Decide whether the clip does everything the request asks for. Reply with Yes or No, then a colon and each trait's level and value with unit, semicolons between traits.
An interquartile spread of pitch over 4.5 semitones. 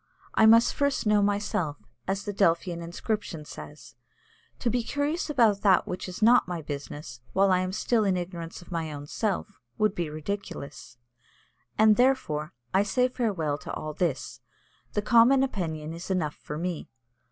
Yes: average, 5.3 semitones